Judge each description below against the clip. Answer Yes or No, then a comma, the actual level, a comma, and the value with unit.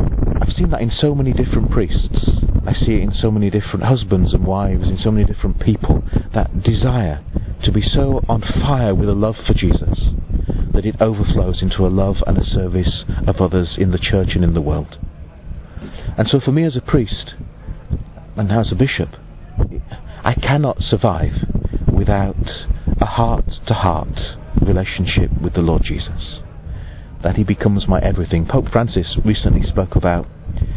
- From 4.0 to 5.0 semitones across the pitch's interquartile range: Yes, average, 4.3 semitones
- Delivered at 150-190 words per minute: Yes, average, 170 wpm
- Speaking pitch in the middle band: No, very low, 95 Hz